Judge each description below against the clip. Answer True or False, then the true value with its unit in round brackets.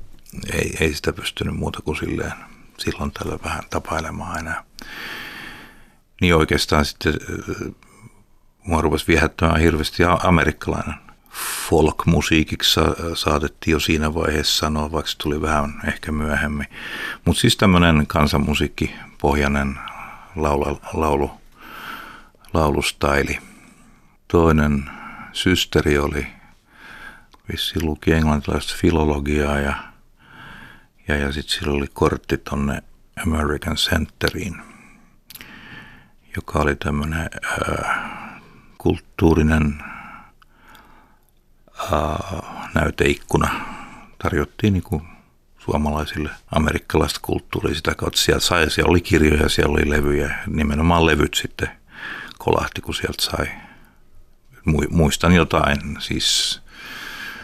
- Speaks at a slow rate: True (90 wpm)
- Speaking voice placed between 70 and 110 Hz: True (75 Hz)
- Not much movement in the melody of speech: True (2.0 semitones)